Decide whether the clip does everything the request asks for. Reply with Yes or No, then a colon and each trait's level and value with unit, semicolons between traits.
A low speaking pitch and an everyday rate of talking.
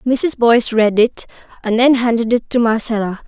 No: high, 230 Hz; average, 185 wpm